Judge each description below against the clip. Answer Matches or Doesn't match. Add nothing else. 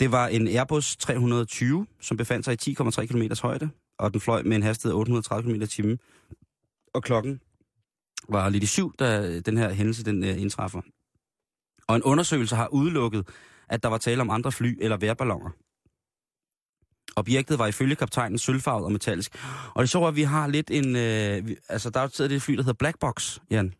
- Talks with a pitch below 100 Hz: Doesn't match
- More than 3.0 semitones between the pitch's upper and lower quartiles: Matches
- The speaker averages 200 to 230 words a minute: Doesn't match